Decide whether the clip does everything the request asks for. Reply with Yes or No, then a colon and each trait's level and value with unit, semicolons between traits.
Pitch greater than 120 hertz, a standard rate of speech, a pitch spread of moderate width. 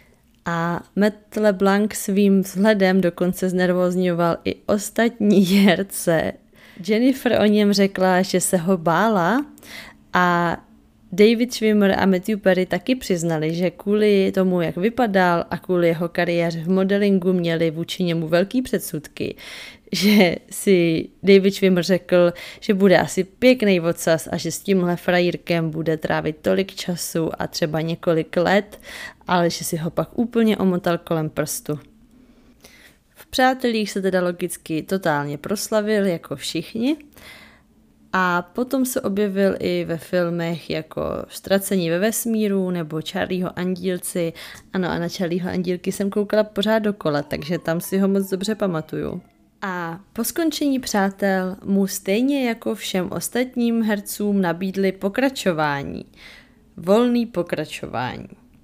Yes: high, 190 Hz; average, 130 wpm; average, 3.4 semitones